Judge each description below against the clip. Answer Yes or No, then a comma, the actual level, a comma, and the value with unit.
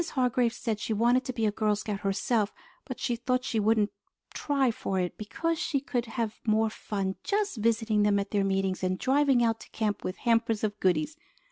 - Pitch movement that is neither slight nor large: Yes, average, 3.2 semitones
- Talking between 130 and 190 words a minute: No, fast, 205 wpm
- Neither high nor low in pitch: No, high, 225 Hz